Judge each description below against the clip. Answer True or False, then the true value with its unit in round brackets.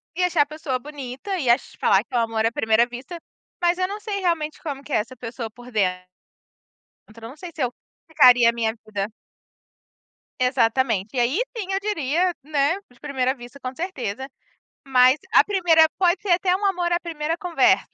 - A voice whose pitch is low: False (275 Hz)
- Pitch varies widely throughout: True (6.4 semitones)